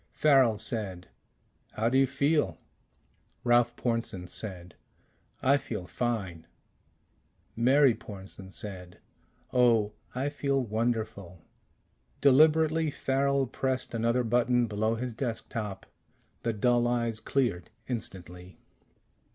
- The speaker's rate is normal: No, slow, 100 wpm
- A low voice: Yes, low, 115 Hz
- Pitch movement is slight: No, average, 4.3 semitones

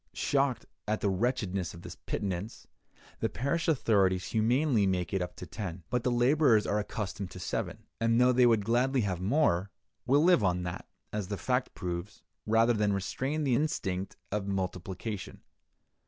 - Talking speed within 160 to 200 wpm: Yes, average, 170 wpm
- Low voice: Yes, low, 105 Hz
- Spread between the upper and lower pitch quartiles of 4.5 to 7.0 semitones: Yes, average, 4.8 semitones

